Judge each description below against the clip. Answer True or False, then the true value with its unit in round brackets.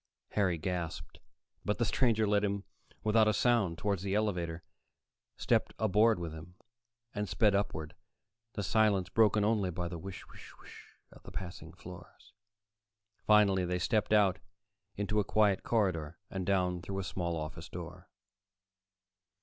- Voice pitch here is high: False (95 Hz)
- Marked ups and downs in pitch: False (3.3 semitones)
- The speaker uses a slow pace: False (150 wpm)